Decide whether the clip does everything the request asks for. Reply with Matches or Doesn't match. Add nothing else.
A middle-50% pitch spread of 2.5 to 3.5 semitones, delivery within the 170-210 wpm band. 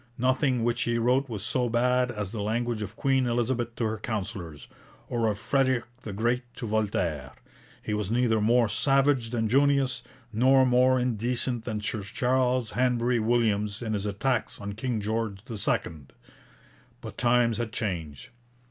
Doesn't match